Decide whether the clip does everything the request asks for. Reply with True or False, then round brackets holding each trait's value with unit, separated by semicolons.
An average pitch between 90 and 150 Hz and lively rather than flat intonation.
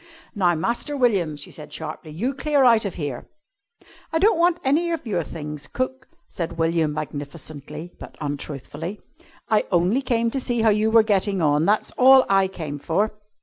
False (195 Hz; 7.9 semitones)